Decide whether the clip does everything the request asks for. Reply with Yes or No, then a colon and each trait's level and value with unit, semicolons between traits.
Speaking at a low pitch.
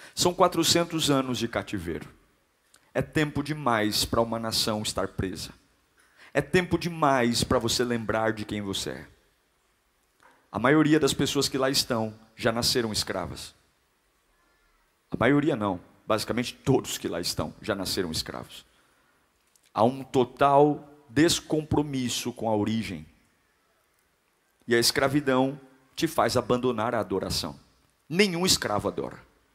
Yes: low, 125 Hz